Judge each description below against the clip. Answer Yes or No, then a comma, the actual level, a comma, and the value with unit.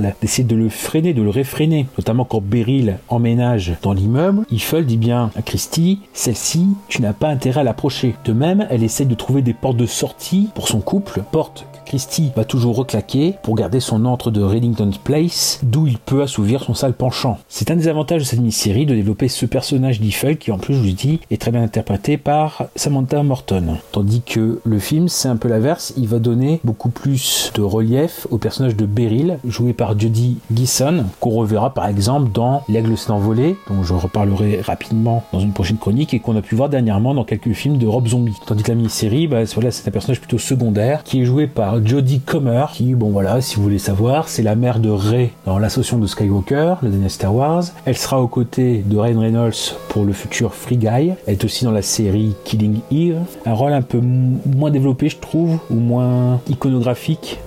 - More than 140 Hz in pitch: No, low, 120 Hz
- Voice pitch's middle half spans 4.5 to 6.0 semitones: No, average, 3.9 semitones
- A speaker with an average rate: Yes, average, 210 wpm